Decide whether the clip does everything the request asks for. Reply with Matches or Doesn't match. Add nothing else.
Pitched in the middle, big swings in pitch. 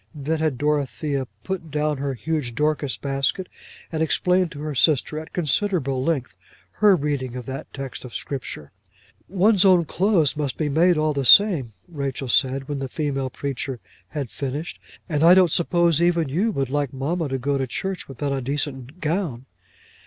Doesn't match